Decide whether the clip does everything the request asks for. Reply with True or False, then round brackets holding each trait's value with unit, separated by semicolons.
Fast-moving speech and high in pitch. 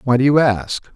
False (255 wpm; 130 Hz)